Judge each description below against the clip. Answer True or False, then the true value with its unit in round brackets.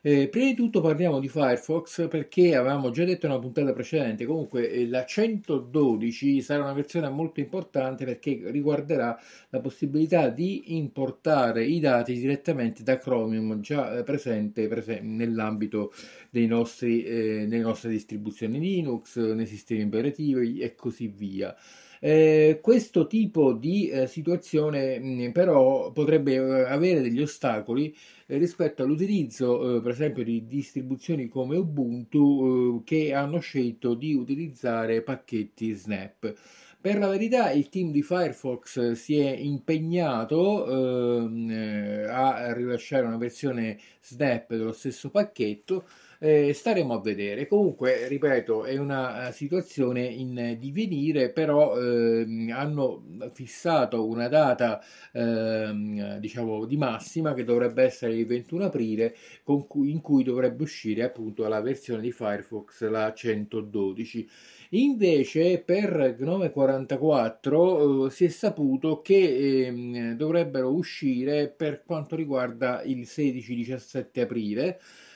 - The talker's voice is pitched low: True (130 Hz)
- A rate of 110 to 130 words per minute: True (125 wpm)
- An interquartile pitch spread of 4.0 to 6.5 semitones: True (4.9 semitones)